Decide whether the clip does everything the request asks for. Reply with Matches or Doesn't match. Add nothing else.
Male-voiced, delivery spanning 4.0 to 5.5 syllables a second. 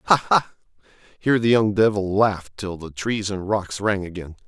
Matches